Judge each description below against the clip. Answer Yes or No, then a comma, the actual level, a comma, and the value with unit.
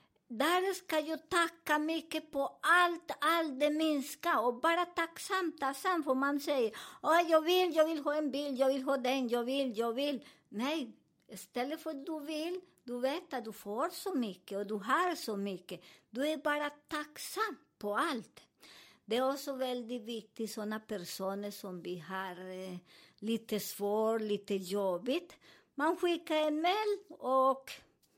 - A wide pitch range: Yes, wide, 6.5 semitones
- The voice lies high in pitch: Yes, very high, 275 Hz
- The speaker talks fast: No, average, 165 wpm